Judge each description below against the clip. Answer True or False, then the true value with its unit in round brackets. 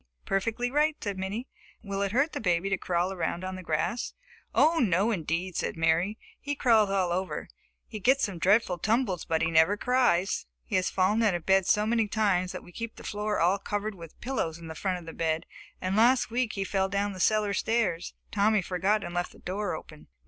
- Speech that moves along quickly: True (215 wpm)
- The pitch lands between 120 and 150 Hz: False (195 Hz)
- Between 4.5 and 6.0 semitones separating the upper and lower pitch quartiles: False (3.6 semitones)